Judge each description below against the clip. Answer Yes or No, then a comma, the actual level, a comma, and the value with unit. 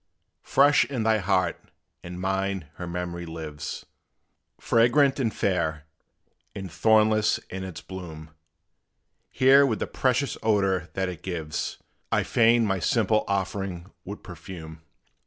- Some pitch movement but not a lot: Yes, average, 4.2 semitones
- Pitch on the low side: Yes, very low, 95 Hz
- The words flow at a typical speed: No, slow, 125 wpm